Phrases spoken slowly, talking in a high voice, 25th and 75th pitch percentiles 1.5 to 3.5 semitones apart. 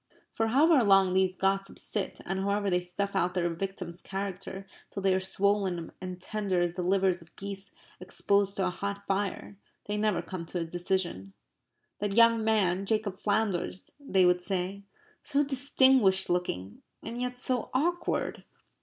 No: average, 165 wpm; high, 195 Hz; narrow, 2.5 semitones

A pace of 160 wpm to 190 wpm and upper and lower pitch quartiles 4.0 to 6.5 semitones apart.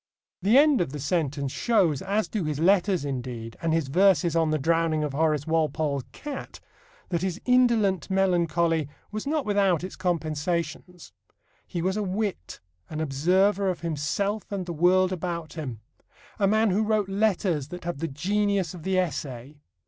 Yes: average, 165 wpm; average, 4.3 semitones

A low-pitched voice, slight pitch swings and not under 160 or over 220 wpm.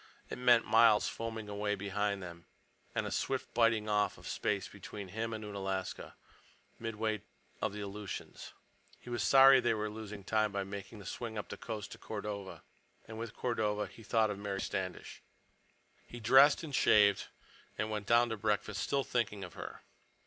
Yes: low, 105 Hz; narrow, 2.1 semitones; average, 175 wpm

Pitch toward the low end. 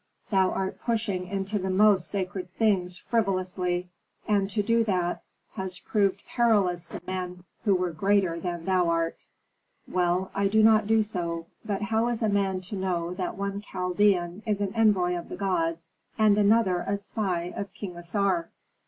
No: high, 190 Hz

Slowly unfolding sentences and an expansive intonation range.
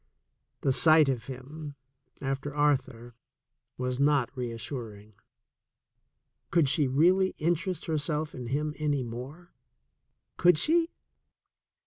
No: slow, 100 wpm; average, 3.6 semitones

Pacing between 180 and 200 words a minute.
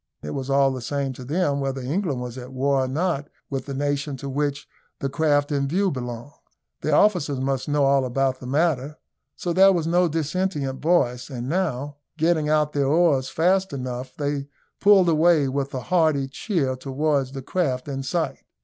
Yes: average, 185 wpm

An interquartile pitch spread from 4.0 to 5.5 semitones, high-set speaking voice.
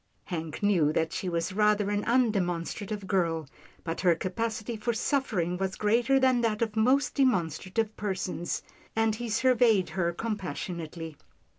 Yes: average, 4.6 semitones; high, 205 Hz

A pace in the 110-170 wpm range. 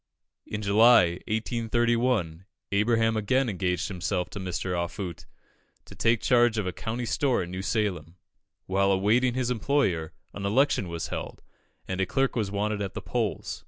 Yes: average, 160 wpm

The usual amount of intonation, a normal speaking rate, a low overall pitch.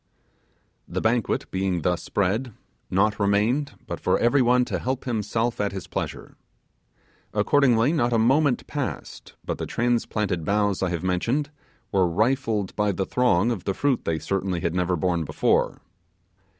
Yes: average, 4.7 semitones; average, 150 wpm; low, 105 Hz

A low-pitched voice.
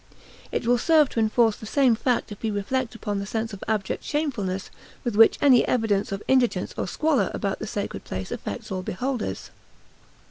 No: high, 225 Hz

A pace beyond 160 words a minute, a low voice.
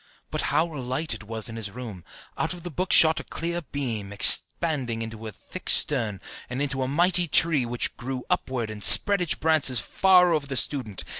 Yes: average, 200 wpm; low, 130 Hz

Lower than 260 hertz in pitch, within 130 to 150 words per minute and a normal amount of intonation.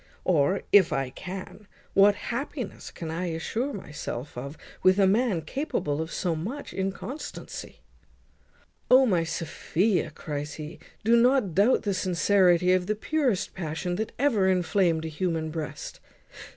Yes: medium, 185 Hz; average, 140 wpm; average, 4.7 semitones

